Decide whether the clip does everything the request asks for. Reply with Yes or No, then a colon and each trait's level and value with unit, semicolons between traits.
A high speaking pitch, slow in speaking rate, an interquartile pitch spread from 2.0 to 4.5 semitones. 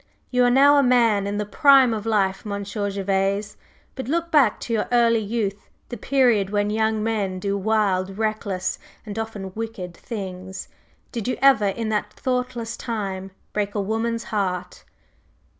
No: high, 215 Hz; average, 160 wpm; average, 2.8 semitones